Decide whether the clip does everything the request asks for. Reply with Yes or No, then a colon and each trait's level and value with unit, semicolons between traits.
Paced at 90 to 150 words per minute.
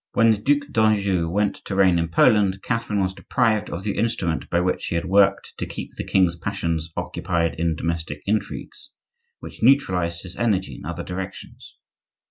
No: average, 175 wpm